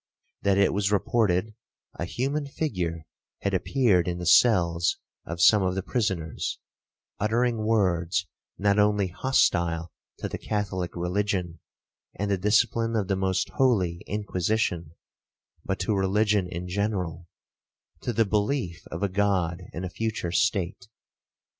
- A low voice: Yes, very low, 95 Hz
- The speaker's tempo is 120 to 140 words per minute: Yes, slow, 135 wpm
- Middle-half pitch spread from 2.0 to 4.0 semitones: Yes, average, 3.3 semitones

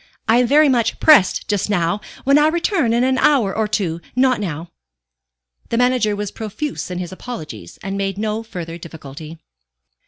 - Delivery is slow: No, average, 175 wpm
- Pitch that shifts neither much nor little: No, wide, 5.9 semitones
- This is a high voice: Yes, high, 210 Hz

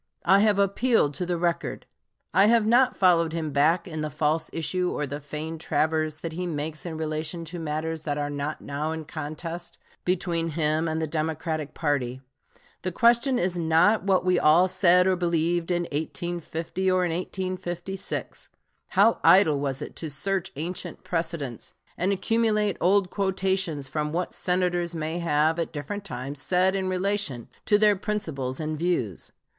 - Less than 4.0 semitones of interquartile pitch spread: Yes, average, 3.2 semitones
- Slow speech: No, average, 165 wpm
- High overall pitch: No, medium, 170 Hz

